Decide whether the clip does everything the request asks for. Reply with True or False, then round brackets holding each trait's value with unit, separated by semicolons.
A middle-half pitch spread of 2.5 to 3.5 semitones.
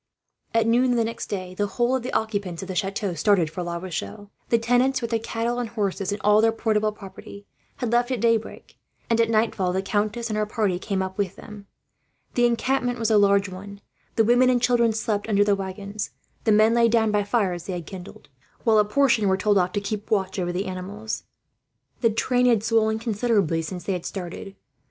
True (2.9 semitones)